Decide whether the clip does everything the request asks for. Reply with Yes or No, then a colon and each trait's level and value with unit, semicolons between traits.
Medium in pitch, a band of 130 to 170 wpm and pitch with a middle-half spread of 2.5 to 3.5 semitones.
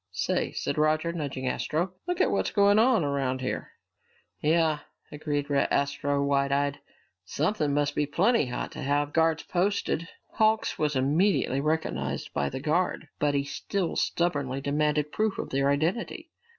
Yes: medium, 150 Hz; average, 150 wpm; average, 3.2 semitones